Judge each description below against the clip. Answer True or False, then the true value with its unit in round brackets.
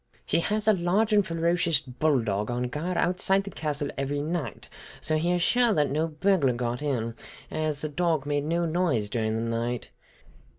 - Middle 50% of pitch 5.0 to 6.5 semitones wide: True (5.6 semitones)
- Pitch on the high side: False (155 Hz)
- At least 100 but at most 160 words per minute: False (175 wpm)